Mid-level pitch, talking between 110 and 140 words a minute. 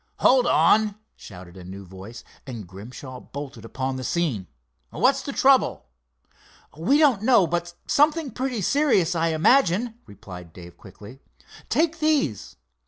Yes: medium, 160 Hz; slow, 135 wpm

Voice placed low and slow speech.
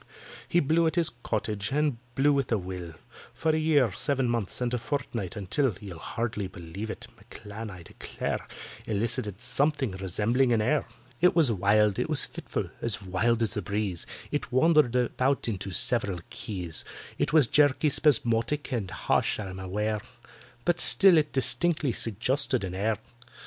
No: low, 115 Hz; average, 155 wpm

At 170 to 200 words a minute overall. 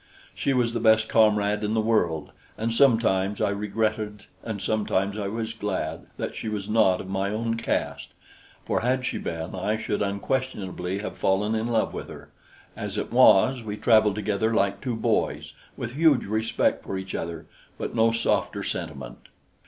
Yes: average, 175 wpm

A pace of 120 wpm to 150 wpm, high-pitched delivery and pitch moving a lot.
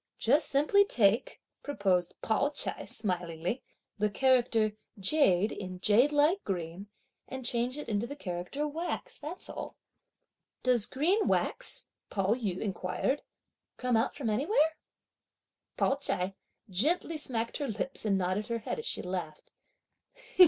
Yes: slow, 135 wpm; high, 230 Hz; wide, 6.8 semitones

